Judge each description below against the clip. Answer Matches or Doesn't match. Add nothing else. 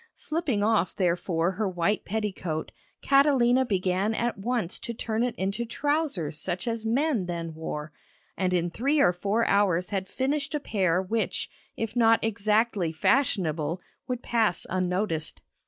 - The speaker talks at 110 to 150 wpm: Matches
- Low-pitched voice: Doesn't match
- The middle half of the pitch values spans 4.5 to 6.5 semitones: Matches